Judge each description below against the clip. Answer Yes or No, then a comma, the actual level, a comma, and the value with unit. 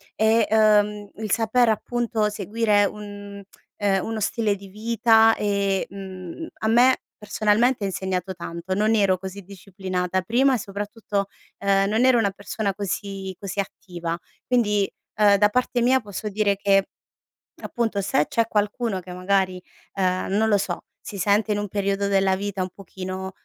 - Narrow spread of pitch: Yes, narrow, 2.2 semitones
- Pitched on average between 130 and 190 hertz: No, high, 200 Hz